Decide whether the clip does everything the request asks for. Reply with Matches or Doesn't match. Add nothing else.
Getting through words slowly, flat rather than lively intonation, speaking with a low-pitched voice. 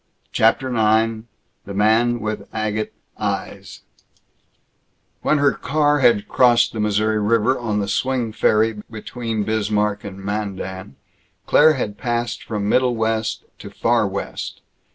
Matches